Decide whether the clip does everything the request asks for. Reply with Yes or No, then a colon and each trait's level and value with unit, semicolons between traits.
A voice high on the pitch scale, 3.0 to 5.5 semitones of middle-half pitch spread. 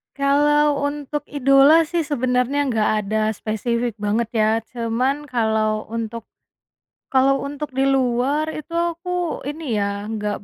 Yes: very high, 260 Hz; average, 4.7 semitones